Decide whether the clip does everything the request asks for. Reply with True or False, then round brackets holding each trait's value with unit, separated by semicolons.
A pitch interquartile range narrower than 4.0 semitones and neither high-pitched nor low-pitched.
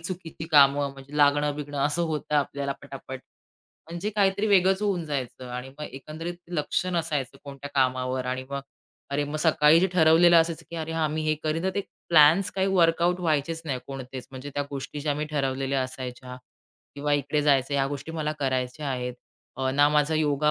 True (3.0 semitones; 150 Hz)